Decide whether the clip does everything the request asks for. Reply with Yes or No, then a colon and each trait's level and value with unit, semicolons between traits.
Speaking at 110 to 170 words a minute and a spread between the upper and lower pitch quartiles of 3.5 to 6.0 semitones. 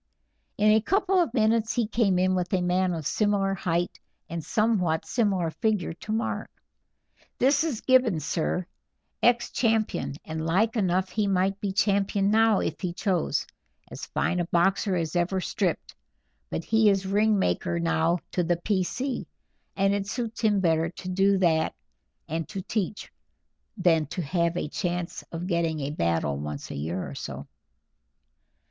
Yes: average, 165 wpm; average, 4.1 semitones